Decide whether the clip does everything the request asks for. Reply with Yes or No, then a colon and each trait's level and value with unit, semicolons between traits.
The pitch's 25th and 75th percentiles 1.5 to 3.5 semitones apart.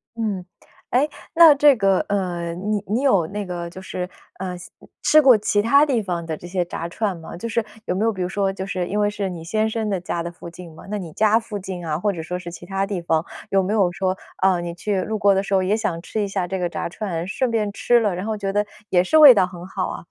Yes: average, 3.1 semitones